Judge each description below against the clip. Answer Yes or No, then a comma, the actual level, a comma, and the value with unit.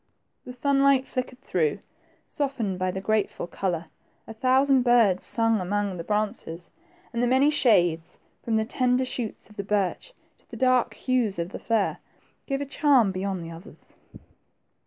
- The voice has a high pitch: Yes, high, 220 Hz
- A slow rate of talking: No, average, 160 wpm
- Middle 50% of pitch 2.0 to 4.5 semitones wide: No, average, 5.2 semitones